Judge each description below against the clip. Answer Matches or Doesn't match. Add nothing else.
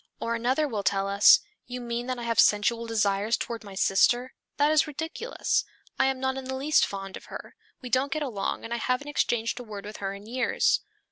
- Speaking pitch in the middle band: Doesn't match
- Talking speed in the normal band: Doesn't match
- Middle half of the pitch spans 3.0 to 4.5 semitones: Matches